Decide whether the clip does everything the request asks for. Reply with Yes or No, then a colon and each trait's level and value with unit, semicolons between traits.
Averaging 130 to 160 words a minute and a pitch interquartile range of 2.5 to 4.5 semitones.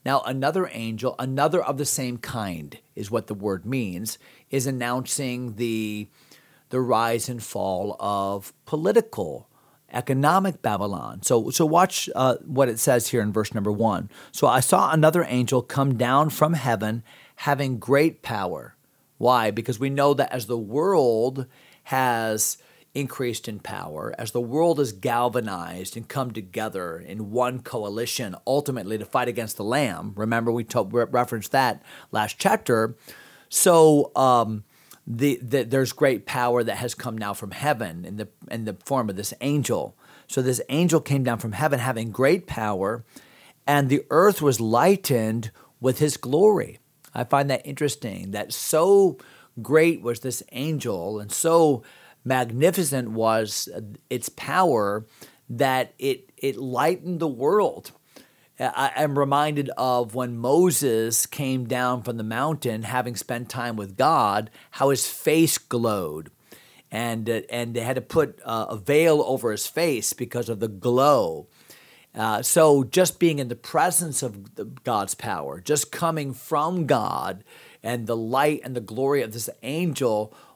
Yes: average, 150 wpm; average, 3.8 semitones